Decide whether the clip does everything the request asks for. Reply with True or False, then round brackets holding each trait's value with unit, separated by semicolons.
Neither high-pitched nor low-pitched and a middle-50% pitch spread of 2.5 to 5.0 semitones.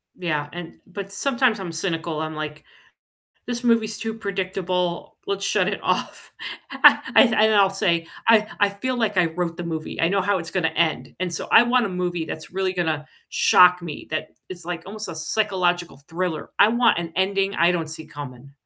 True (180 Hz; 3.5 semitones)